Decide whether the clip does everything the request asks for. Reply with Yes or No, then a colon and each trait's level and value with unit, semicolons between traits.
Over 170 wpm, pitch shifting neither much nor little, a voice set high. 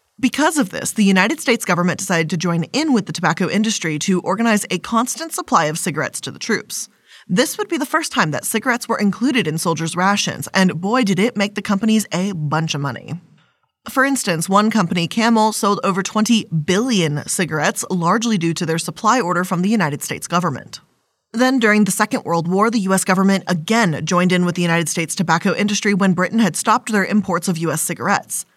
Yes: fast, 205 wpm; average, 4.6 semitones; high, 195 Hz